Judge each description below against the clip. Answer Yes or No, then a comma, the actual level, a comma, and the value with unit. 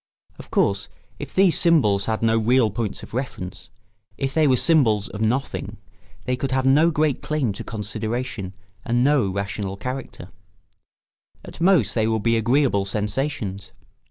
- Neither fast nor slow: Yes, average, 155 wpm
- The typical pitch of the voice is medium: No, low, 115 Hz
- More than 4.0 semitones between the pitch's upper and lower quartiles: Yes, average, 4.6 semitones